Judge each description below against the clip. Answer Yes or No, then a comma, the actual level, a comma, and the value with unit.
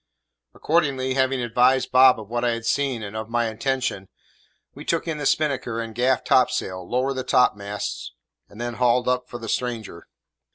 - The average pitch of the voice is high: No, low, 125 Hz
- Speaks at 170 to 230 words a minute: Yes, average, 175 wpm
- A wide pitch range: No, narrow, 2.5 semitones